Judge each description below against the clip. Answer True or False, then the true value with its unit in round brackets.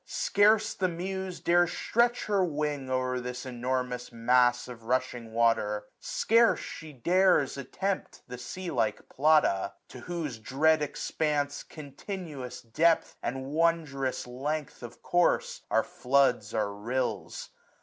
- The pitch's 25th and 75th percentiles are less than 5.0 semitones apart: False (5.3 semitones)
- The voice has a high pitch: False (140 Hz)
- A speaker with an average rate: False (130 wpm)